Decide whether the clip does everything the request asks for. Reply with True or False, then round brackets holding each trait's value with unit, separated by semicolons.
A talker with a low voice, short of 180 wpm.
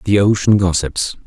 True (95 Hz; 140 wpm)